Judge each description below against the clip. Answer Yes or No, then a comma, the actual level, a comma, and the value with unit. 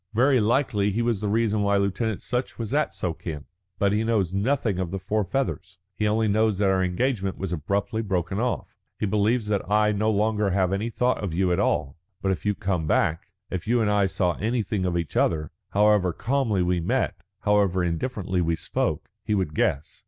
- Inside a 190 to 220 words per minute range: Yes, fast, 205 wpm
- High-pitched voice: No, low, 100 Hz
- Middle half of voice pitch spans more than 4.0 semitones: No, average, 3.1 semitones